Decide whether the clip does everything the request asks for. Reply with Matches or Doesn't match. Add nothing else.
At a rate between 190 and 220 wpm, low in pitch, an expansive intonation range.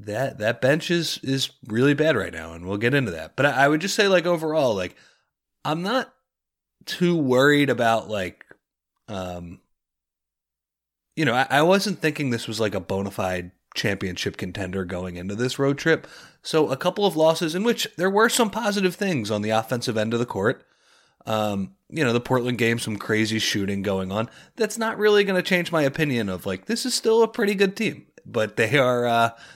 Matches